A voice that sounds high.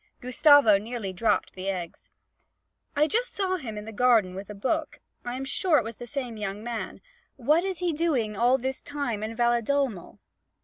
Yes: high, 240 Hz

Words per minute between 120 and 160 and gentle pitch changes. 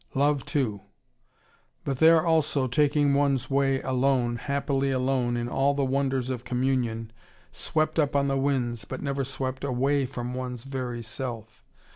Yes: average, 150 wpm; narrow, 2.1 semitones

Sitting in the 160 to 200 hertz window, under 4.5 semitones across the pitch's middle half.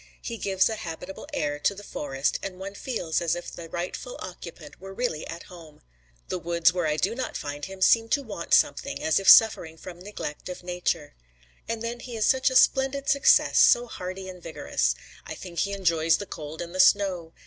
Yes: medium, 185 Hz; average, 4.1 semitones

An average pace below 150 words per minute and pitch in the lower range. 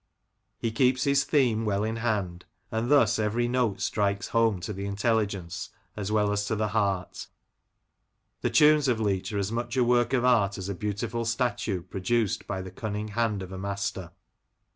No: average, 185 wpm; low, 105 Hz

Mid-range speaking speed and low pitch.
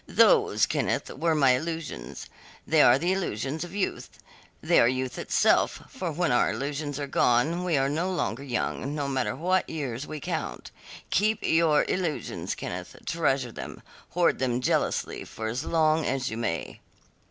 No: average, 165 wpm; medium, 145 Hz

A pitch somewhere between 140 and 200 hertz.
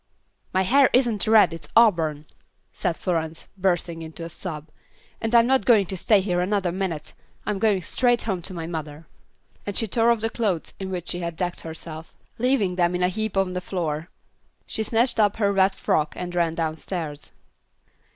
Yes: medium, 185 Hz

